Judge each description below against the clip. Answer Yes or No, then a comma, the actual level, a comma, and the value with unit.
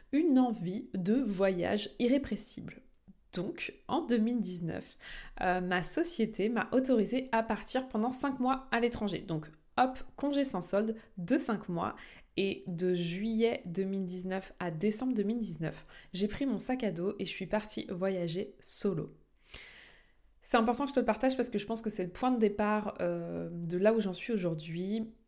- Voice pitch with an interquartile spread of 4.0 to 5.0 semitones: Yes, average, 4.5 semitones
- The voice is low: No, high, 210 Hz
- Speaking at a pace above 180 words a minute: No, average, 170 wpm